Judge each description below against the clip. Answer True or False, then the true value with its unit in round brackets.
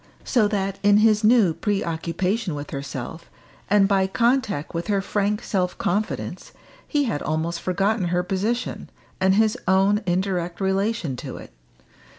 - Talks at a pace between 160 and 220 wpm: False (145 wpm)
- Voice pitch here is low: False (195 Hz)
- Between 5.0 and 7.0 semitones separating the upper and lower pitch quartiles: False (3.2 semitones)